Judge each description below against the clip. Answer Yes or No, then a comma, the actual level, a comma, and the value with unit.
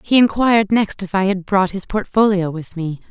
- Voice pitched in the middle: No, high, 195 Hz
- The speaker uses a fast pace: Yes, fast, 215 wpm